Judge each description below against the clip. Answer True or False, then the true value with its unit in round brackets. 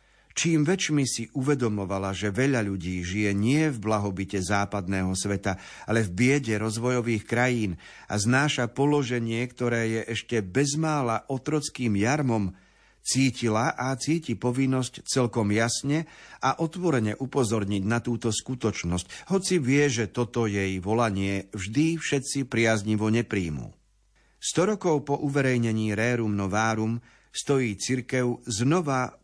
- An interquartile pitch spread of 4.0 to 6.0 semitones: True (4.4 semitones)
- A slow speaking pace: False (120 wpm)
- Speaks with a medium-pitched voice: False (120 Hz)